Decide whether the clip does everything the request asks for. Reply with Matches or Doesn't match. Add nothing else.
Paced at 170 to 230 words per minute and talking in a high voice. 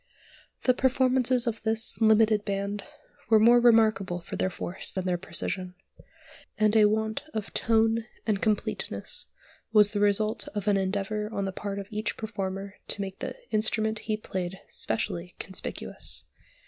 Doesn't match